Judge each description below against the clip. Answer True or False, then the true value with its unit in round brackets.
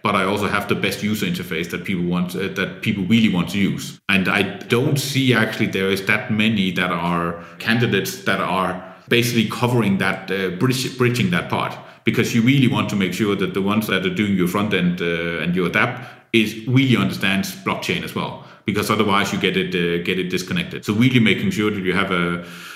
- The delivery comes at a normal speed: False (220 wpm)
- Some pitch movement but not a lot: True (3.5 semitones)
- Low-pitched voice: True (100 Hz)